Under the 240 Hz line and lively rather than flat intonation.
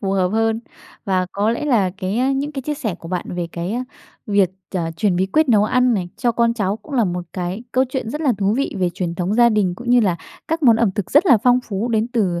No: high, 215 Hz; average, 4.8 semitones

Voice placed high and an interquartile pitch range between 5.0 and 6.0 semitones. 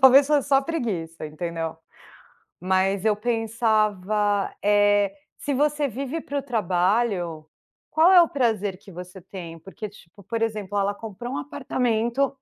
Yes: high, 215 Hz; wide, 5.5 semitones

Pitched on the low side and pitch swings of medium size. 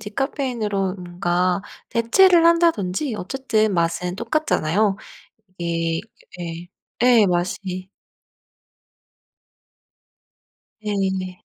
No: high, 195 Hz; average, 4.7 semitones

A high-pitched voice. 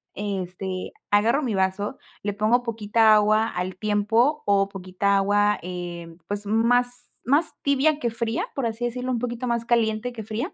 Yes: high, 215 Hz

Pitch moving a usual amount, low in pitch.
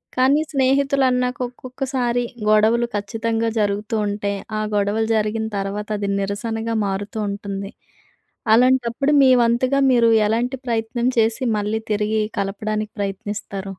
No: average, 3.2 semitones; high, 225 Hz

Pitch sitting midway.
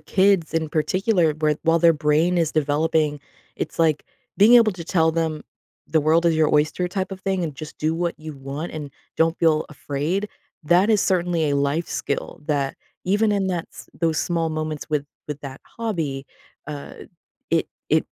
Yes: medium, 160 Hz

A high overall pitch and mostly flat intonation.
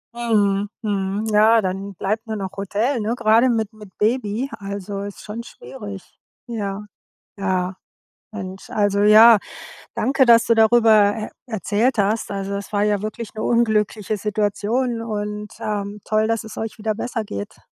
Yes: high, 210 Hz; narrow, 2.0 semitones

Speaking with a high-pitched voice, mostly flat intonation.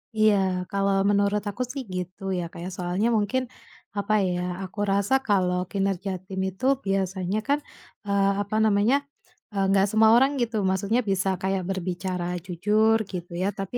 Yes: high, 195 Hz; narrow, 2.0 semitones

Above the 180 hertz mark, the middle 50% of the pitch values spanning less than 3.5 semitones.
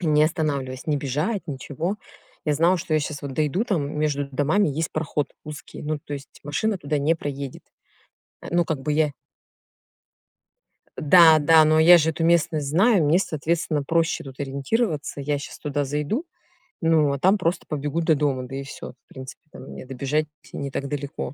No: medium, 150 Hz; narrow, 2.6 semitones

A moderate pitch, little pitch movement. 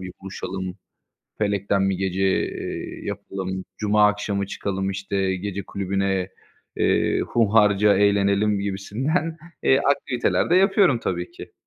No: low, 100 Hz; narrow, 1.6 semitones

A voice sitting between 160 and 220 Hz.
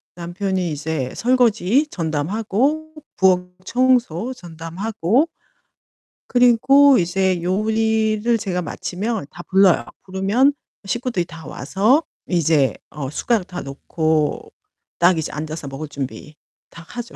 Yes: high, 190 Hz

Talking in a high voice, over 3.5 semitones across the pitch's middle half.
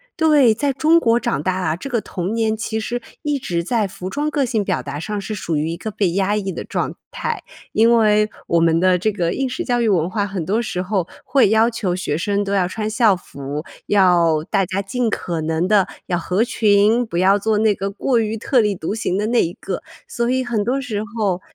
Yes: high, 205 Hz; average, 4.1 semitones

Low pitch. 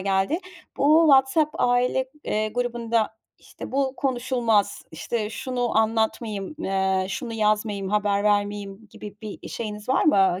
No: high, 220 Hz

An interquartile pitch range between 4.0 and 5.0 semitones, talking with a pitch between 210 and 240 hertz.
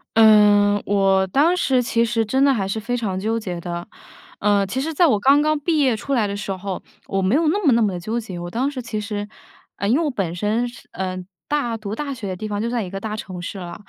Yes: average, 4.5 semitones; high, 215 Hz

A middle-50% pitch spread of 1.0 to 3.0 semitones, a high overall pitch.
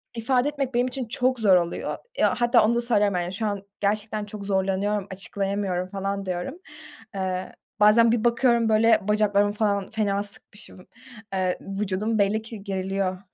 Yes: narrow, 2.6 semitones; high, 205 Hz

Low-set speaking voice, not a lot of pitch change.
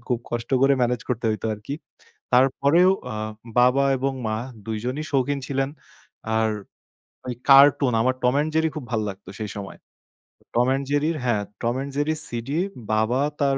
No: low, 130 Hz; average, 3.1 semitones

